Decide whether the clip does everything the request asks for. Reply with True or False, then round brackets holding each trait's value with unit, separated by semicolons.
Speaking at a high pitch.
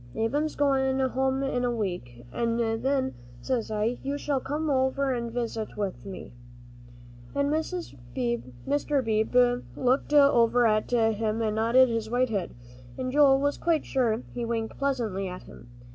True (245 Hz)